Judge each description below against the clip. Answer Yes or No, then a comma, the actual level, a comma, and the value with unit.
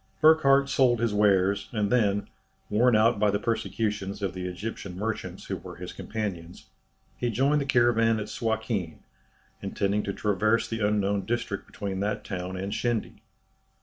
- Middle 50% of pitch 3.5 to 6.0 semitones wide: No, average, 2.8 semitones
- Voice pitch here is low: Yes, low, 105 Hz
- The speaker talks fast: No, average, 155 wpm